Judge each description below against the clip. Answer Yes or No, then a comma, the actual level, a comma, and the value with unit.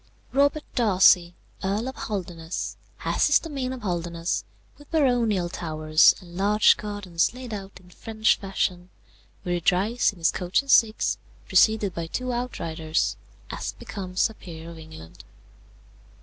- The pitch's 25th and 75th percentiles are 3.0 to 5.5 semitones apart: Yes, average, 4.9 semitones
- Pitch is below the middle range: No, high, 195 Hz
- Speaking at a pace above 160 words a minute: No, average, 145 wpm